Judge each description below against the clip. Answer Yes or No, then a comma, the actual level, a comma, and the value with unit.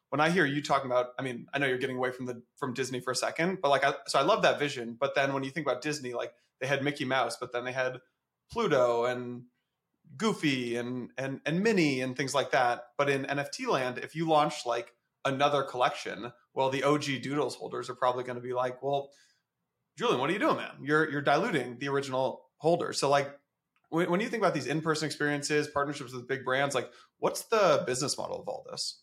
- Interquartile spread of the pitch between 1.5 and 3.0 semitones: Yes, narrow, 2.5 semitones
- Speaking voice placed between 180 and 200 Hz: No, medium, 140 Hz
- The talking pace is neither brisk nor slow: No, fast, 230 wpm